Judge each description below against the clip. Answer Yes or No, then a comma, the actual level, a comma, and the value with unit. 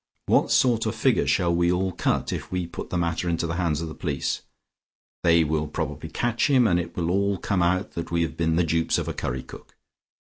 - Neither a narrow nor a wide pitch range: No, narrow, 2.1 semitones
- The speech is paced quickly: Yes, fast, 235 wpm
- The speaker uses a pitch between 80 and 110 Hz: Yes, very low, 85 Hz